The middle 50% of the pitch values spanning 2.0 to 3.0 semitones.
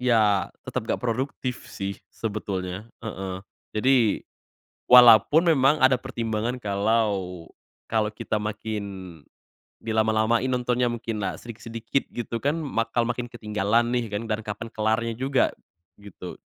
Yes: average, 2.7 semitones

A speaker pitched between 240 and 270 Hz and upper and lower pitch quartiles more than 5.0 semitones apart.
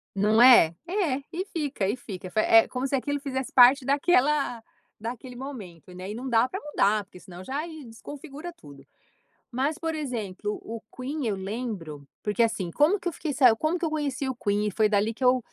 Yes: very high, 250 Hz; wide, 5.4 semitones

